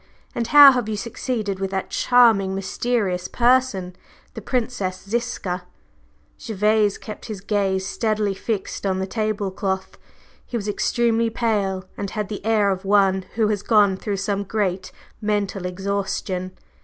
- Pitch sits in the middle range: No, high, 205 Hz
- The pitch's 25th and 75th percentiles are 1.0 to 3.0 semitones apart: Yes, narrow, 2.6 semitones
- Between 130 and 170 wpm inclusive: Yes, average, 145 wpm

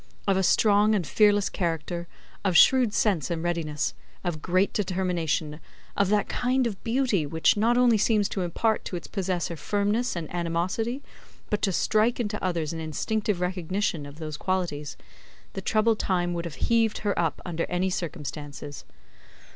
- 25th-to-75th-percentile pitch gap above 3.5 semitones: Yes, average, 4.1 semitones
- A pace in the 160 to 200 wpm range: Yes, average, 165 wpm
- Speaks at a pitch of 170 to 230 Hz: Yes, medium, 185 Hz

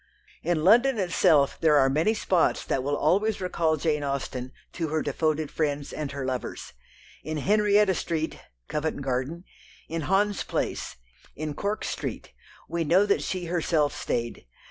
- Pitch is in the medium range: Yes, medium, 160 Hz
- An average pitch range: Yes, average, 4.4 semitones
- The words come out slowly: No, average, 150 wpm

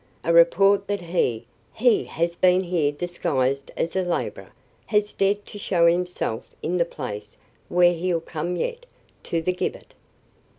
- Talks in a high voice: No, medium, 175 Hz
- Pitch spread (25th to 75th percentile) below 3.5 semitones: Yes, narrow, 2.4 semitones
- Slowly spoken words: No, average, 155 wpm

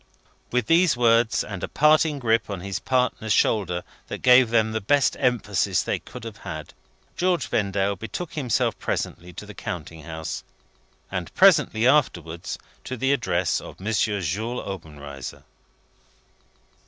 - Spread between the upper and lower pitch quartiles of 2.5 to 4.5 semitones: No, wide, 5.4 semitones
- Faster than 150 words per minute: No, average, 140 wpm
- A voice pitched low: Yes, low, 110 Hz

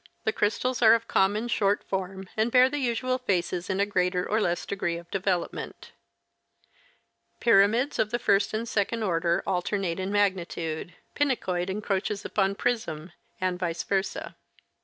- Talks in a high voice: Yes, high, 195 Hz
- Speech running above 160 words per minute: No, average, 155 wpm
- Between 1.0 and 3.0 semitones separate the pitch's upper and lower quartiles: No, average, 3.7 semitones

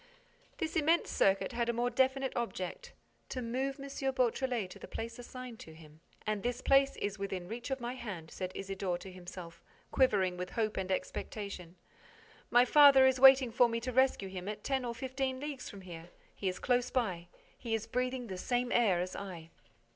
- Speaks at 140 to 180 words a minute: No, average, 190 wpm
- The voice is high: Yes, high, 235 Hz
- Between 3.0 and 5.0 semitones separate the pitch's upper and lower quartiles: No, wide, 5.4 semitones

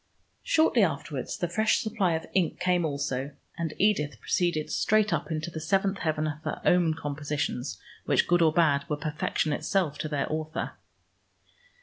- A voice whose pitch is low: No, medium, 160 Hz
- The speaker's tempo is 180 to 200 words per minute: No, average, 160 wpm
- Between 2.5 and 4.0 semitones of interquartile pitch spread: Yes, average, 3.2 semitones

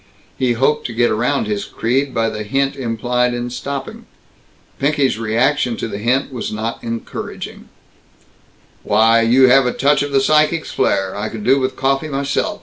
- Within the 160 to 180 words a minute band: Yes, average, 170 wpm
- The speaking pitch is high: No, low, 125 Hz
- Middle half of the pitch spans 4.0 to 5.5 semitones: No, average, 3.2 semitones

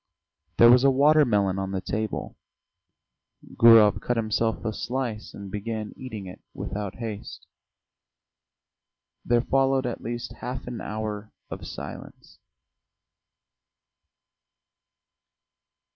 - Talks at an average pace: No, slow, 105 wpm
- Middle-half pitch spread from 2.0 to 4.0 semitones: Yes, average, 2.9 semitones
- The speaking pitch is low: Yes, low, 115 Hz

